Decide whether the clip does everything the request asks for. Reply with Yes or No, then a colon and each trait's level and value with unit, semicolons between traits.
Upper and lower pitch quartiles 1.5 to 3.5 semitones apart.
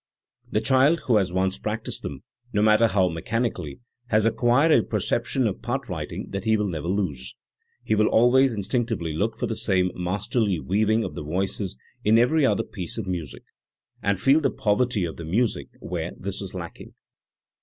No: average, 4.1 semitones